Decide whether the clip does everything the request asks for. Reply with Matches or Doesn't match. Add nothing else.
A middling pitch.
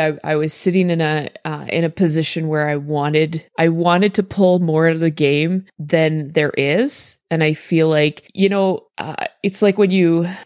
Matches